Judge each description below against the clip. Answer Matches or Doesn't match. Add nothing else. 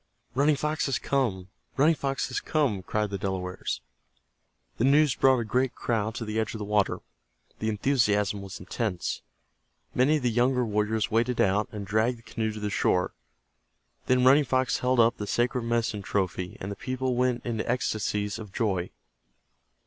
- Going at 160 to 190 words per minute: Matches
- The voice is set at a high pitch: Doesn't match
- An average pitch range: Matches